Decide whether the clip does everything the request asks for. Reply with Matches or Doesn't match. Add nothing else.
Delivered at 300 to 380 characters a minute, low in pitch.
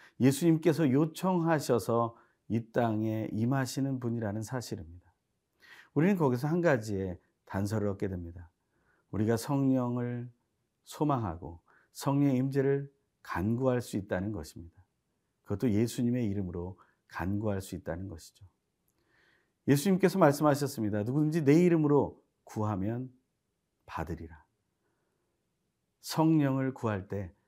Doesn't match